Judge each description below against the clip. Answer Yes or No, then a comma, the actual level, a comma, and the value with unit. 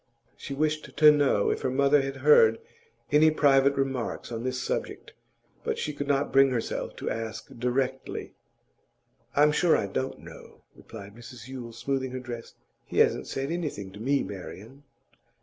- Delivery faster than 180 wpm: No, average, 165 wpm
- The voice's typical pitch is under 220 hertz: Yes, low, 135 Hz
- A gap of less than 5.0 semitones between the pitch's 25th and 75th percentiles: Yes, average, 3.4 semitones